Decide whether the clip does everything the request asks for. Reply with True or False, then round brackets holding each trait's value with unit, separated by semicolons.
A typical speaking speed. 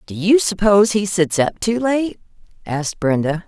True (175 wpm)